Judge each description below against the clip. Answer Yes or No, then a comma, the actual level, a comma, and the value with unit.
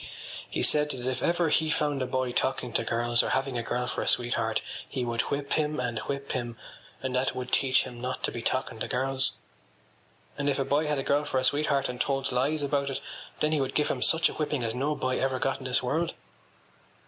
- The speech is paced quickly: Yes, fast, 240 wpm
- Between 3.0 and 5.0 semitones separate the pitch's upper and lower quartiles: No, narrow, 2.4 semitones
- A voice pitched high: No, low, 130 Hz